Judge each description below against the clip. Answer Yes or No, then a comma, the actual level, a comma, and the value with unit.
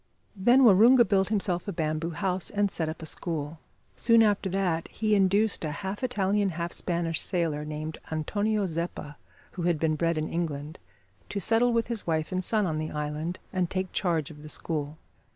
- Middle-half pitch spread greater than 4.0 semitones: Yes, average, 4.4 semitones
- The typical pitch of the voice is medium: Yes, medium, 175 Hz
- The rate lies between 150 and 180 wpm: No, average, 190 wpm